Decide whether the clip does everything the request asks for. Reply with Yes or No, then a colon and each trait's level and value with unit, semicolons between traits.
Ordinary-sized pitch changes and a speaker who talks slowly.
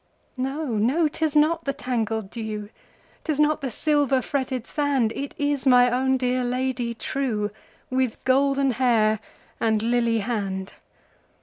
Yes: average, 3.6 semitones; slow, 120 wpm